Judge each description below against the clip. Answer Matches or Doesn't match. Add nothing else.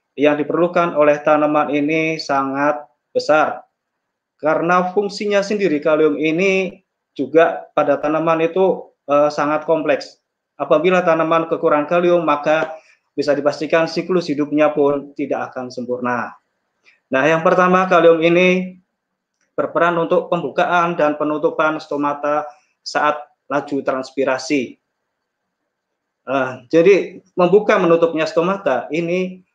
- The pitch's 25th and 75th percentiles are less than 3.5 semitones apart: Matches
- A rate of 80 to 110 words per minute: Matches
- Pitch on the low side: Doesn't match